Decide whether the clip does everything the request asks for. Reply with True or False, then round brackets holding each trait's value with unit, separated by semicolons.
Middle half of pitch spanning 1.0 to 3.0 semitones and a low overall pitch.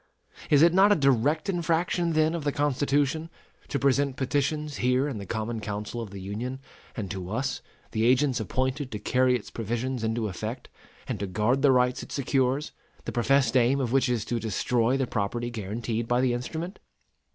False (3.9 semitones; 125 Hz)